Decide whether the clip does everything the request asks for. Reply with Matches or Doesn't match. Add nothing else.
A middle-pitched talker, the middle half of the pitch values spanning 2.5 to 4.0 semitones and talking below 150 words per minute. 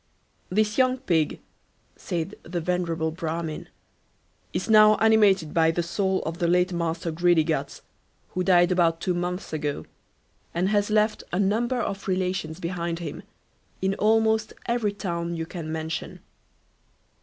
Matches